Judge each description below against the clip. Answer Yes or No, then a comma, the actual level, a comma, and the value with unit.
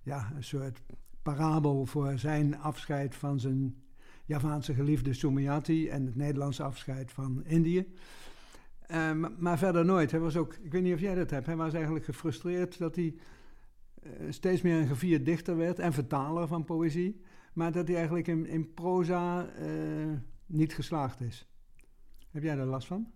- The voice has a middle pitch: Yes, medium, 155 Hz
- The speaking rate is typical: Yes, average, 170 wpm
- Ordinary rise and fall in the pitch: Yes, average, 3.3 semitones